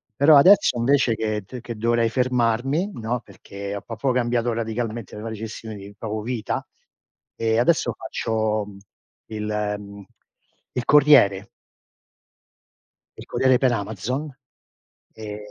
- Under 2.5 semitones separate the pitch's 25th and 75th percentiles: No, average, 2.8 semitones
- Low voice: Yes, low, 115 Hz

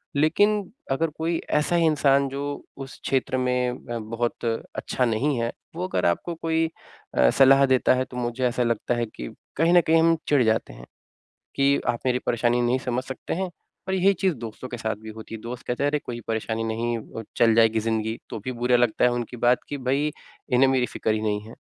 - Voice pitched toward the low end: Yes, low, 125 Hz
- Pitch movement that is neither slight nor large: Yes, average, 3.6 semitones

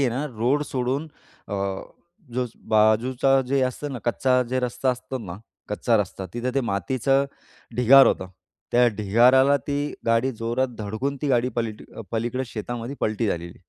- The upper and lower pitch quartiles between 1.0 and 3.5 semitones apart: Yes, average, 2.9 semitones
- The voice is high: No, low, 125 Hz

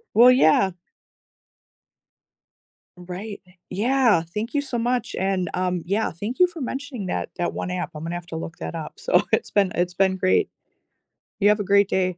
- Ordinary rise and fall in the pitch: Yes, average, 4.5 semitones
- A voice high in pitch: Yes, high, 195 Hz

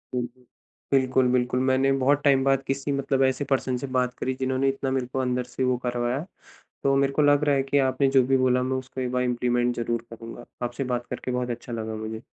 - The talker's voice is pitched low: Yes, low, 130 Hz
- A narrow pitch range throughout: Yes, narrow, 1.7 semitones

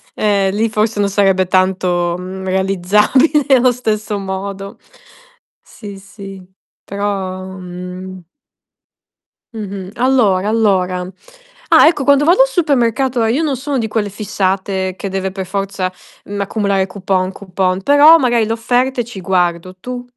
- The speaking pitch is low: No, high, 200 Hz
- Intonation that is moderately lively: Yes, average, 3.7 semitones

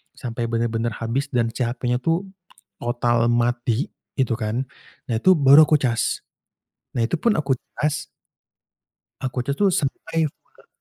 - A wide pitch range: No, average, 3.6 semitones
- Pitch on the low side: Yes, low, 125 Hz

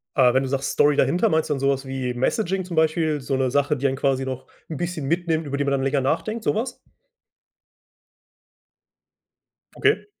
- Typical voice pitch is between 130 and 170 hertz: Yes, medium, 140 Hz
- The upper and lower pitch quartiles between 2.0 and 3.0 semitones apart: No, average, 3.5 semitones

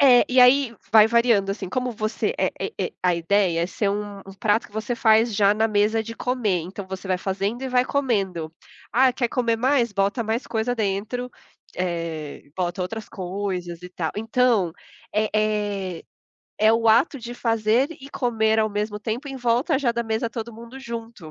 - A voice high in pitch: Yes, high, 220 Hz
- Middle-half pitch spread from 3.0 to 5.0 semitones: Yes, average, 3.4 semitones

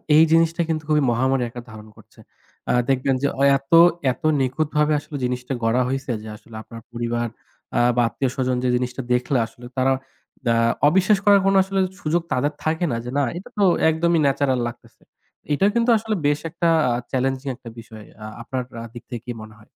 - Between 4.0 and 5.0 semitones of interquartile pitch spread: Yes, average, 4.4 semitones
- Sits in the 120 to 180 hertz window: Yes, low, 135 Hz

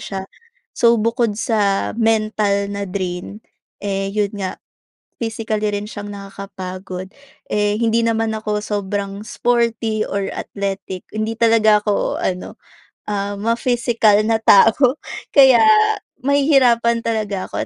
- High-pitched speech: Yes, high, 215 Hz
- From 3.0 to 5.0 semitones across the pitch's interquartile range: No, narrow, 2.4 semitones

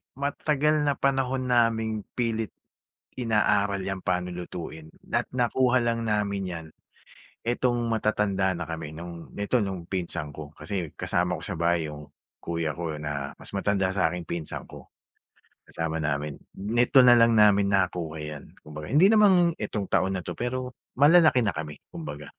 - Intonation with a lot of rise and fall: Yes, wide, 6.4 semitones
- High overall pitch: No, low, 100 Hz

